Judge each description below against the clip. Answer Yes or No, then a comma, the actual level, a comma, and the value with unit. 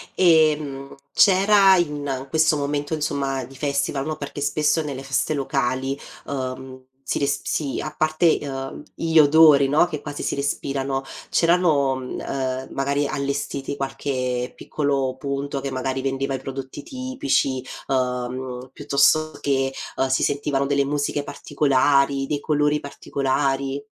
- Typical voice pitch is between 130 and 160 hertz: Yes, medium, 140 Hz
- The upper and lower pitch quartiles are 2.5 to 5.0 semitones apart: No, narrow, 1.7 semitones